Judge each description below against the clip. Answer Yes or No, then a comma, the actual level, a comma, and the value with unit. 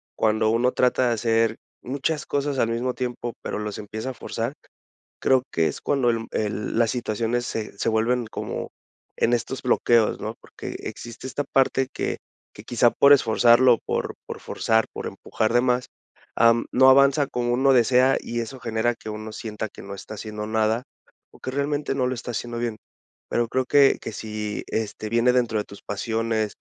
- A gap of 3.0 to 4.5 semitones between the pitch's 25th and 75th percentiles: No, narrow, 2.5 semitones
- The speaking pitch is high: No, low, 120 Hz